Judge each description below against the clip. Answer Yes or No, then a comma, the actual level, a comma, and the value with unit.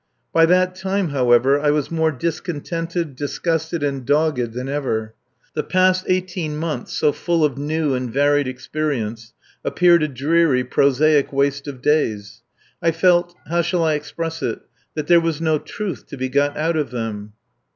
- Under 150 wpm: No, average, 165 wpm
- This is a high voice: No, medium, 150 Hz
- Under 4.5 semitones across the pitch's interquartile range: Yes, average, 3.8 semitones